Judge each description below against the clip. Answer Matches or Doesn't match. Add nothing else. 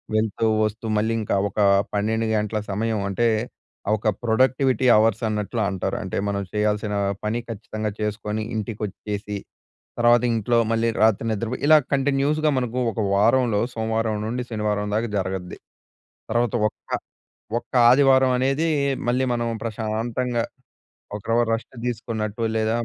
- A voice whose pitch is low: Matches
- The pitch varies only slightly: Matches